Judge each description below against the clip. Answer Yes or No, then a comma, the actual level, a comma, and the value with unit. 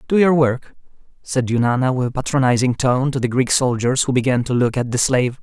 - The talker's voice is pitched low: Yes, low, 130 Hz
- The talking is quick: Yes, fast, 220 wpm